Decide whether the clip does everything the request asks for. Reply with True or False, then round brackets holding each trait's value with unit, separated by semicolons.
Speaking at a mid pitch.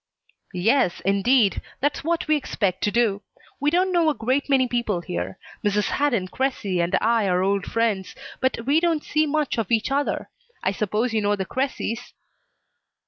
False (230 Hz)